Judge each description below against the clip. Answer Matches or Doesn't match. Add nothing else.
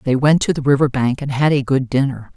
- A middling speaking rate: Doesn't match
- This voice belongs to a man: Doesn't match